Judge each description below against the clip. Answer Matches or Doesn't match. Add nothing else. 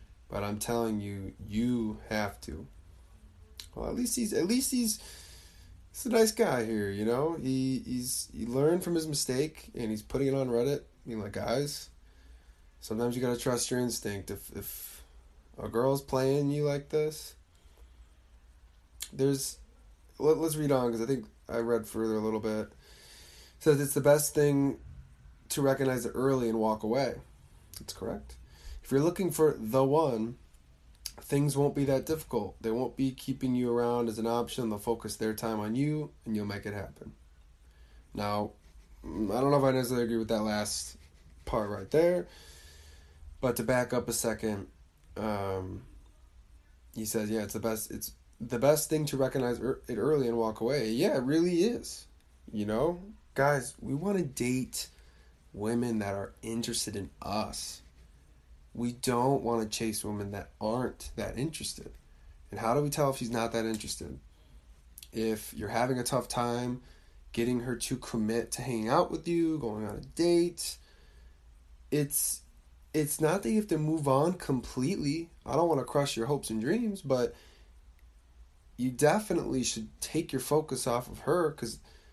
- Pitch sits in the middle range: Doesn't match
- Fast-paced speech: Doesn't match